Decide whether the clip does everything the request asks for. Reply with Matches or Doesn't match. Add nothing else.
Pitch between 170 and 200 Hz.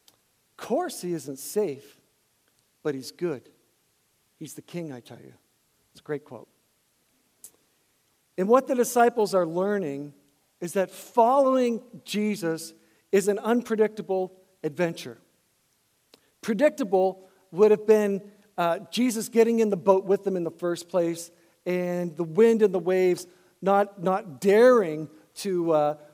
Matches